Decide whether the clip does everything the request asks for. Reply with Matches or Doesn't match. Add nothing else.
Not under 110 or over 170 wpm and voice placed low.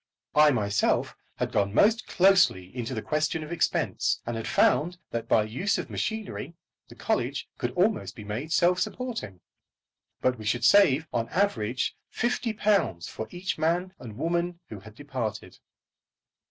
Doesn't match